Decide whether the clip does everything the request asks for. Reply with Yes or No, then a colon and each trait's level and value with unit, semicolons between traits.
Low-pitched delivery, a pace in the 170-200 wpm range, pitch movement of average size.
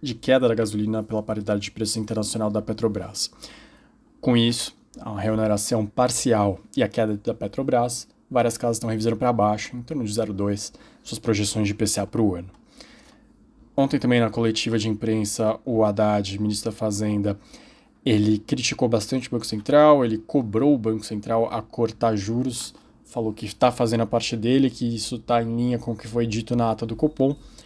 No: low, 115 Hz; average, 180 wpm; narrow, 2.0 semitones